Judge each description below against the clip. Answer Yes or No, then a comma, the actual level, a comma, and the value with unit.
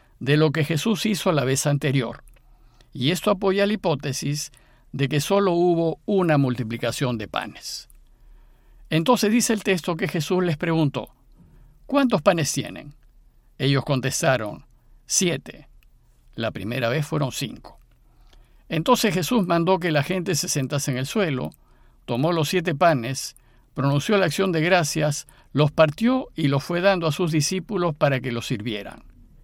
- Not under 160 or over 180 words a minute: No, average, 150 wpm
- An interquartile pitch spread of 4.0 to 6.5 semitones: Yes, wide, 5.5 semitones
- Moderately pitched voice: Yes, medium, 155 Hz